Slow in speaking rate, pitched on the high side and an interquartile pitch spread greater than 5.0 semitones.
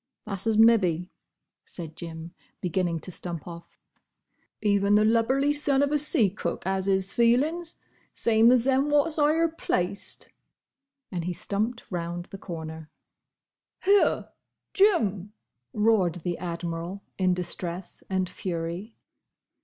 Yes: slow, 125 wpm; high, 195 Hz; wide, 5.4 semitones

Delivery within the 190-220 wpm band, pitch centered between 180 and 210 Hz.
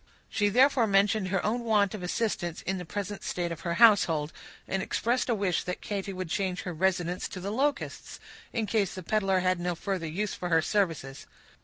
Yes: average, 200 wpm; high, 190 Hz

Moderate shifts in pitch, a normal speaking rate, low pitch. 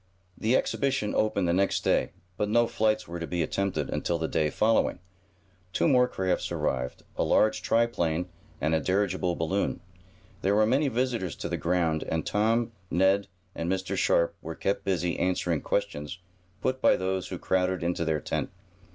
Yes: average, 4.2 semitones; average, 170 wpm; very low, 95 Hz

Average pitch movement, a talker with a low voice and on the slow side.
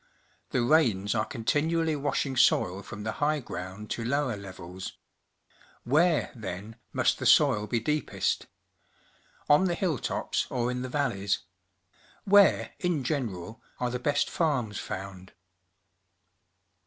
No: wide, 6.3 semitones; low, 125 Hz; slow, 125 wpm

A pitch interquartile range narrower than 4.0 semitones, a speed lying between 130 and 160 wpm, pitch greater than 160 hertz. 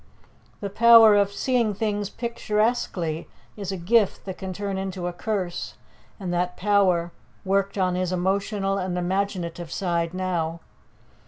Yes: narrow, 2.5 semitones; average, 140 wpm; high, 190 Hz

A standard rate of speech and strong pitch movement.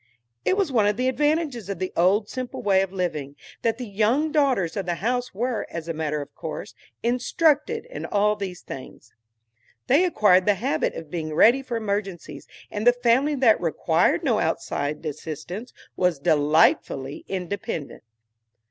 Yes: average, 165 wpm; wide, 6.7 semitones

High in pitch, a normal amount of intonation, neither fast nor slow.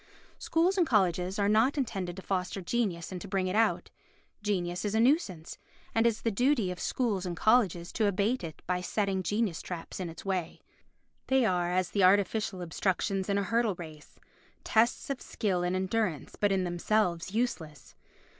Yes: high, 195 Hz; average, 3.7 semitones; average, 180 wpm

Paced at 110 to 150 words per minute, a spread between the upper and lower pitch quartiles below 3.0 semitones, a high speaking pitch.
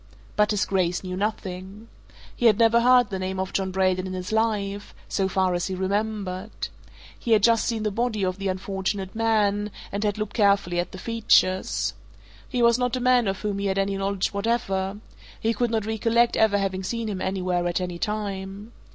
No: average, 200 wpm; narrow, 2.6 semitones; high, 200 Hz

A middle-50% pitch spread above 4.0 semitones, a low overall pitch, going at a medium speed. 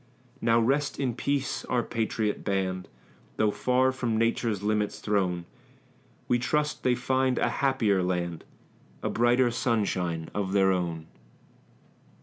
No: average, 4.9 semitones; low, 110 Hz; slow, 130 wpm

